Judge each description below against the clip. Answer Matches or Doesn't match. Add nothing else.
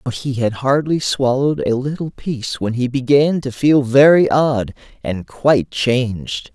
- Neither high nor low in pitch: Doesn't match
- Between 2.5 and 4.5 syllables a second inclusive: Matches